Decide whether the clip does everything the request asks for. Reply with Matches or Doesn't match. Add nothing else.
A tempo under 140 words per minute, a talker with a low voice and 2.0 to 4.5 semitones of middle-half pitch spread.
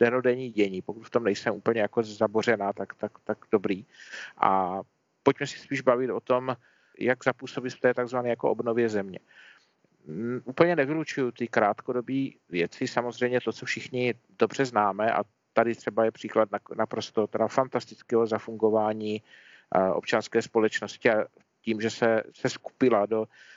Doesn't match